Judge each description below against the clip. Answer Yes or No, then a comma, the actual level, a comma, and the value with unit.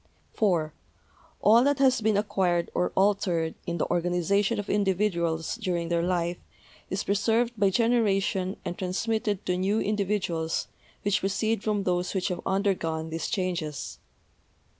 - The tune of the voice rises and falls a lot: No, average, 3.2 semitones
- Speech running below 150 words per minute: Yes, average, 140 wpm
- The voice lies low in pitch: No, high, 190 Hz